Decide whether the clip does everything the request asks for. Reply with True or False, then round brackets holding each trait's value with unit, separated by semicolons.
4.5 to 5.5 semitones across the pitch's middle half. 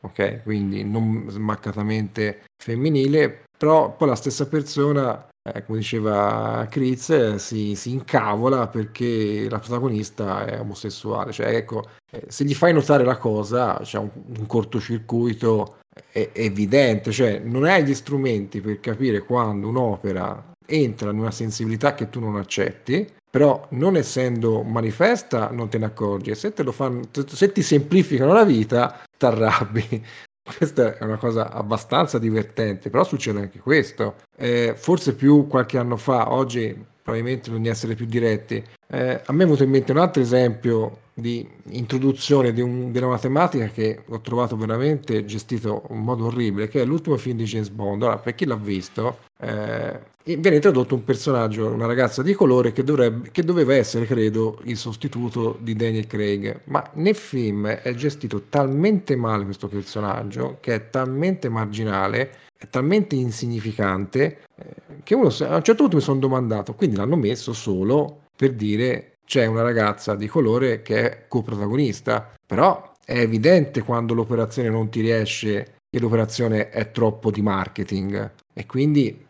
False (4.0 semitones)